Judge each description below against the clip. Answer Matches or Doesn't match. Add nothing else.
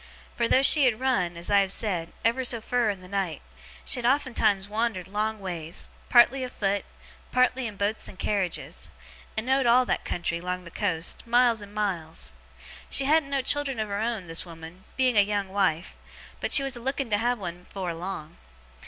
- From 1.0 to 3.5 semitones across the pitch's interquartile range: Doesn't match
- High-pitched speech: Matches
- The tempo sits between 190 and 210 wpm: Matches